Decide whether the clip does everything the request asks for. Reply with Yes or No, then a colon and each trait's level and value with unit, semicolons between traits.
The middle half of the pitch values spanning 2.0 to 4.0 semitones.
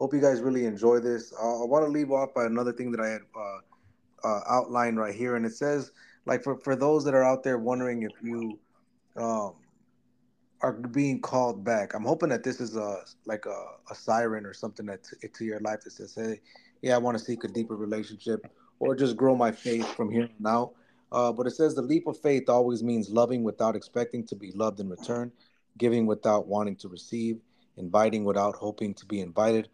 Yes: narrow, 2.4 semitones